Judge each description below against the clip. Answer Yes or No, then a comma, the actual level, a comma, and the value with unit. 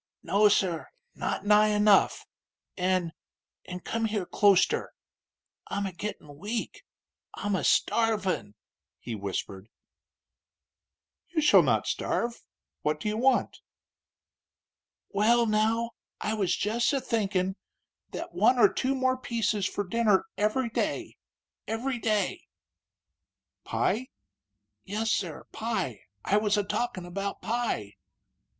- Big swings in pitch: No, average, 3.5 semitones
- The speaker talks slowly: Yes, slow, 120 wpm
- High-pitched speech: Yes, high, 210 Hz